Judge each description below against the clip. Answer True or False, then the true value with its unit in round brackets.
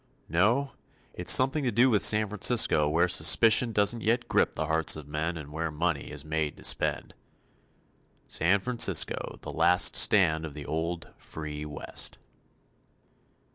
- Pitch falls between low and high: False (85 Hz)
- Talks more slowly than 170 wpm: True (150 wpm)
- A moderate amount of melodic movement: False (5.7 semitones)